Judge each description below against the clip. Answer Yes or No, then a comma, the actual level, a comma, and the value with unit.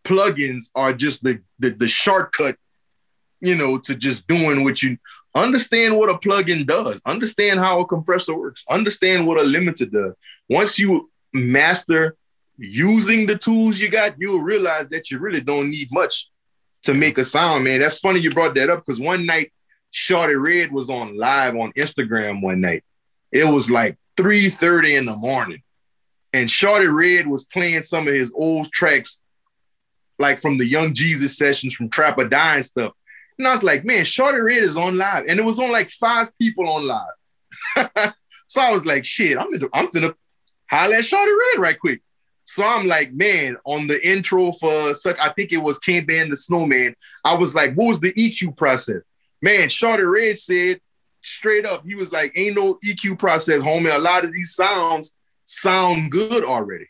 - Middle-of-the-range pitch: Yes, medium, 165 Hz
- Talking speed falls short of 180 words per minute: No, average, 185 wpm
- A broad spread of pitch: Yes, wide, 6.2 semitones